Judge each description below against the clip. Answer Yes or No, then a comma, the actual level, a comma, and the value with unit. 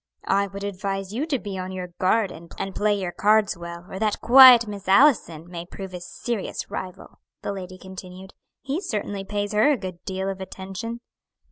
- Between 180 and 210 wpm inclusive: Yes, average, 190 wpm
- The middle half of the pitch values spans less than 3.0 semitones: Yes, narrow, 2.4 semitones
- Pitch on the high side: Yes, high, 195 Hz